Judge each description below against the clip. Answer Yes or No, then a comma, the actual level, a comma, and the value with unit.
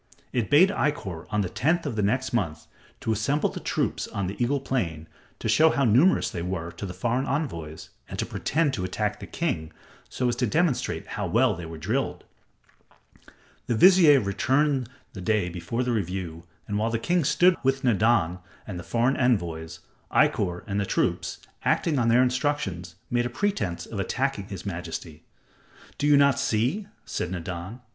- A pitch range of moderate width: No, wide, 7.1 semitones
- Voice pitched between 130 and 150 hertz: No, low, 115 Hz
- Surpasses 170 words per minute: Yes, average, 180 wpm